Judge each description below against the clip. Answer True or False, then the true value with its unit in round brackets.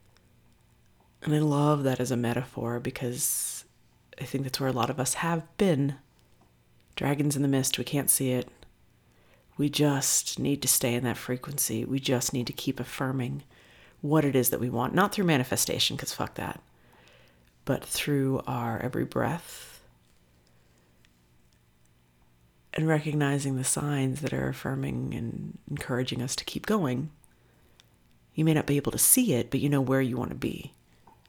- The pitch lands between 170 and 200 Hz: False (125 Hz)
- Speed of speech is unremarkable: True (165 wpm)